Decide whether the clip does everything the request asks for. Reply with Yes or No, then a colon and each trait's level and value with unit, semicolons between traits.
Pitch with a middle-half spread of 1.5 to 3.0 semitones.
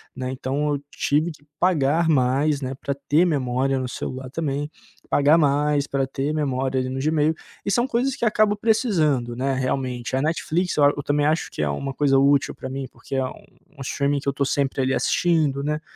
Yes: average, 2.7 semitones